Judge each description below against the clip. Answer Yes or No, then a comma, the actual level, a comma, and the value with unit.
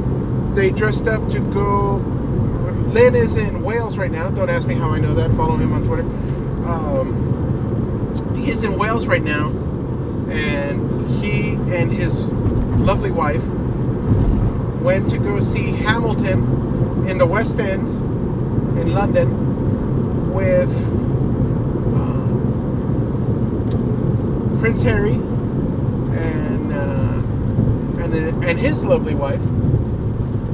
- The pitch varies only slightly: Yes, narrow, 1.3 semitones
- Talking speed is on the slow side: Yes, slow, 110 wpm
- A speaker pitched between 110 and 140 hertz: Yes, low, 120 Hz